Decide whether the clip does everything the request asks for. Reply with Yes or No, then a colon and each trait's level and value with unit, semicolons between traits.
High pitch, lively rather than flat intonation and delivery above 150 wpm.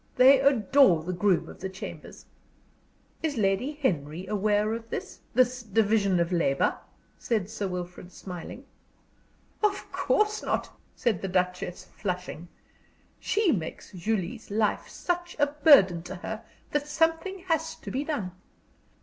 No: high, 215 Hz; wide, 7.7 semitones; slow, 135 wpm